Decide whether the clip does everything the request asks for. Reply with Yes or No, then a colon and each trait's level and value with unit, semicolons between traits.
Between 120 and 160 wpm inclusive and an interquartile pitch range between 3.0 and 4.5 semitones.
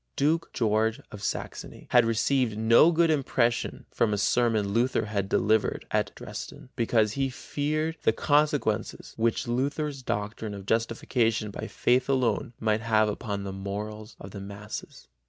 Yes: average, 150 wpm; average, 3.5 semitones